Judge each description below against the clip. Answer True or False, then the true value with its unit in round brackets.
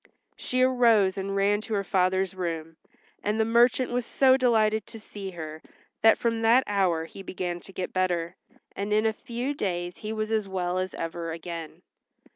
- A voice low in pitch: False (195 Hz)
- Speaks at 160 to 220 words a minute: True (185 wpm)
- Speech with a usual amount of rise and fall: True (4.0 semitones)